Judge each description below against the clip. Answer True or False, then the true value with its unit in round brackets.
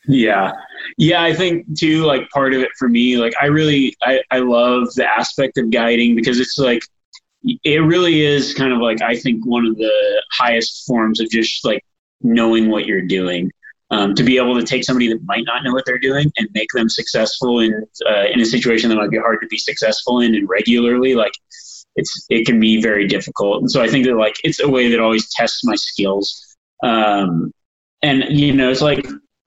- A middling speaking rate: False (210 wpm)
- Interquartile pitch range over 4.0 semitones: False (3.6 semitones)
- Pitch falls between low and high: False (120 Hz)